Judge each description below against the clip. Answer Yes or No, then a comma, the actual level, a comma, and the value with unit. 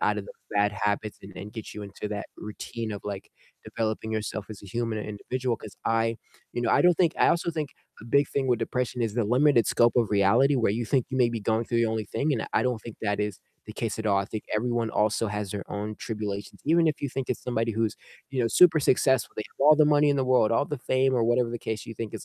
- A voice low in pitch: Yes, low, 115 Hz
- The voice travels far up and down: No, average, 3.4 semitones